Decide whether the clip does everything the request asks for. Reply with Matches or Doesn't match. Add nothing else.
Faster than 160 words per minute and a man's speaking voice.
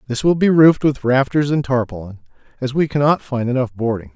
Matches